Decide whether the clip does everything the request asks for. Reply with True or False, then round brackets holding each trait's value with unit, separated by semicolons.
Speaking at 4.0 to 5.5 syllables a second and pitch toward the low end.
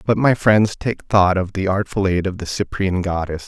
True (4.8 syllables/s; 95 Hz)